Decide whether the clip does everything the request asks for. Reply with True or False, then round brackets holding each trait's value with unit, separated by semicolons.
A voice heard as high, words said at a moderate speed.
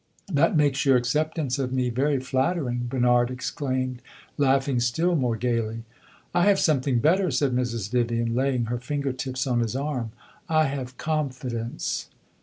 False (130 Hz; 150 wpm)